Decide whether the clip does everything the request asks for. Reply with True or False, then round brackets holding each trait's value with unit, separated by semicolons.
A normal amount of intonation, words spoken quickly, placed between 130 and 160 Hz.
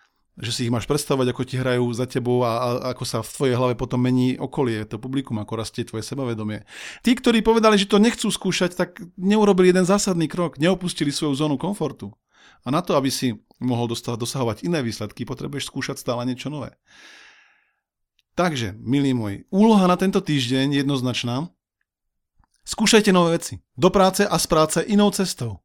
False (6.5 semitones; 175 wpm; 140 Hz)